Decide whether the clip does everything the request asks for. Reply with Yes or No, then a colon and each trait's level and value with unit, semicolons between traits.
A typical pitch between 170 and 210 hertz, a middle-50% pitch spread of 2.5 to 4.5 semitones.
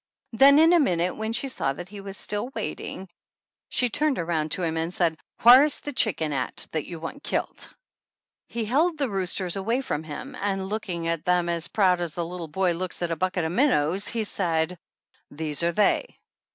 No: medium, 185 Hz; wide, 5.4 semitones